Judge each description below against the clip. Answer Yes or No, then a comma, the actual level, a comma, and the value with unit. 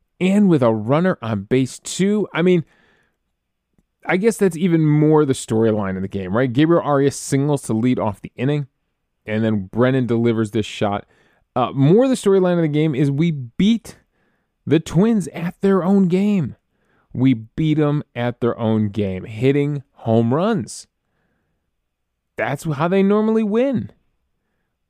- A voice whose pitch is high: No, medium, 140 Hz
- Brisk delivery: No, average, 155 wpm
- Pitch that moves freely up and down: Yes, wide, 8.0 semitones